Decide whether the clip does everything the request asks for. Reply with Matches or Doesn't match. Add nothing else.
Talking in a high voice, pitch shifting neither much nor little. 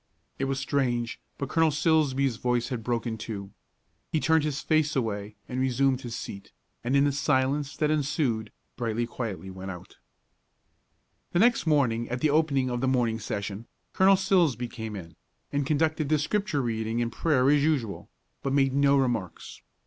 Doesn't match